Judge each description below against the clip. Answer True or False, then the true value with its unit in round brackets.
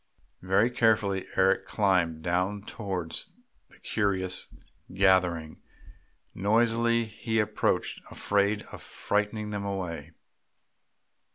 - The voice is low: True (100 Hz)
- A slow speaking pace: True (90 wpm)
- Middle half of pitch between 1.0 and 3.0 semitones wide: True (2.6 semitones)